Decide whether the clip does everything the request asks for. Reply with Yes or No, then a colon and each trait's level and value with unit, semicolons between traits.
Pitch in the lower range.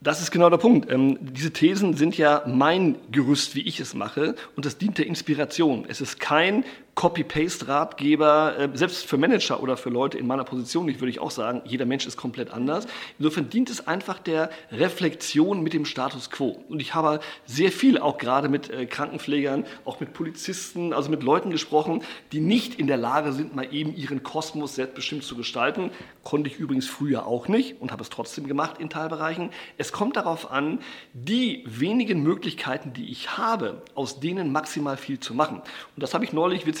No: medium, 155 Hz